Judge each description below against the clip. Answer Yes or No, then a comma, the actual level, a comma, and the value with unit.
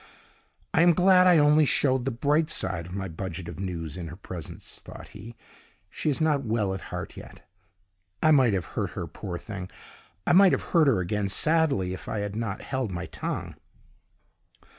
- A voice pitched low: Yes, low, 110 Hz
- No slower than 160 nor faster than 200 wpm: Yes, average, 190 wpm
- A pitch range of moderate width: No, wide, 8.3 semitones